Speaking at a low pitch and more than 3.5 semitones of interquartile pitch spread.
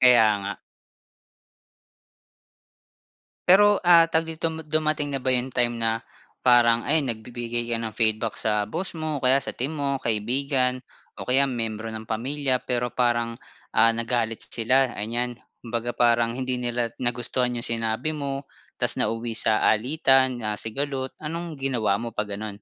No: low, 125 Hz; average, 3.1 semitones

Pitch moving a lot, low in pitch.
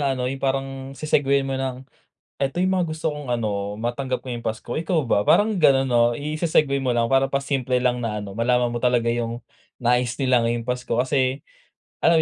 No: narrow, 2.6 semitones; low, 130 Hz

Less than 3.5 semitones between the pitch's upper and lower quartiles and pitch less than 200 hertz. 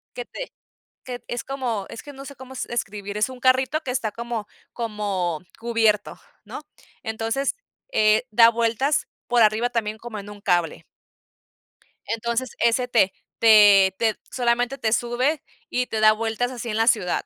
No: narrow, 2.6 semitones; high, 230 Hz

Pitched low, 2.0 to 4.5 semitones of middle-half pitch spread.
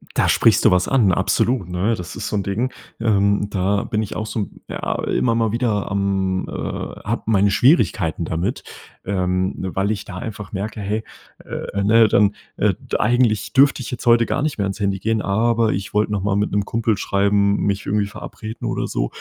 Yes: low, 105 Hz; narrow, 2.4 semitones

